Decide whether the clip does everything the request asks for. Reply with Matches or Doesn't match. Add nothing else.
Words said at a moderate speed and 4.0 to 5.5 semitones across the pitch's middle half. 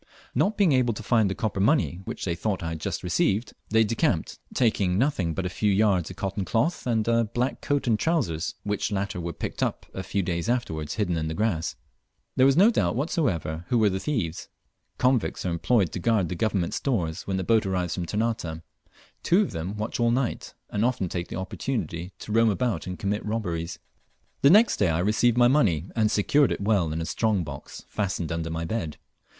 Doesn't match